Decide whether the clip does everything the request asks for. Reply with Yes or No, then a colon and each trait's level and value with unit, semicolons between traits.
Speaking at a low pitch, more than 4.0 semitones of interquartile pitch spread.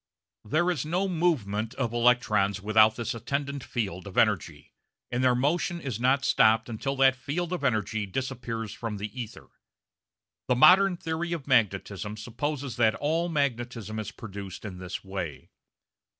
Yes: low, 120 Hz; average, 4.8 semitones